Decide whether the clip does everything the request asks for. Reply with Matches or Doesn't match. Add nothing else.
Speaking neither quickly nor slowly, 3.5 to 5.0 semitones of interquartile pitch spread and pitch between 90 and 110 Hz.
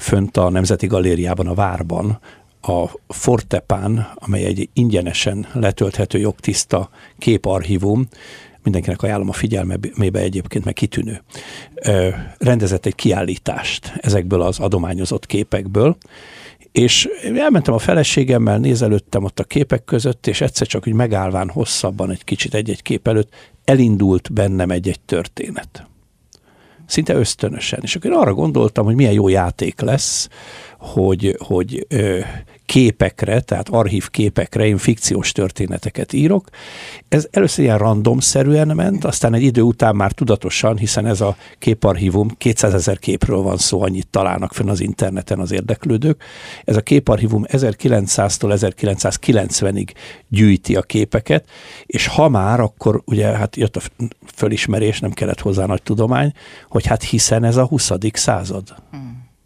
Matches